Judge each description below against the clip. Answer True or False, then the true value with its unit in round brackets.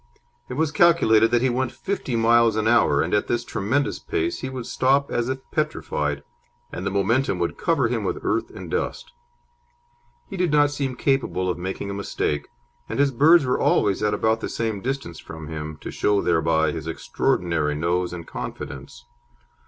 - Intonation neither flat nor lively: False (7.6 semitones)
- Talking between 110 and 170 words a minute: False (185 wpm)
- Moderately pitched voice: False (110 Hz)